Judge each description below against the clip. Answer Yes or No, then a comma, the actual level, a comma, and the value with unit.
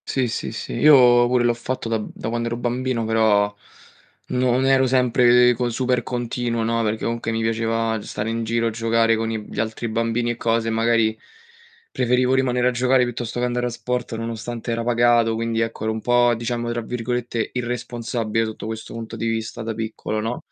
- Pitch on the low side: Yes, low, 115 Hz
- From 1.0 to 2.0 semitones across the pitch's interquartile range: Yes, narrow, 1.5 semitones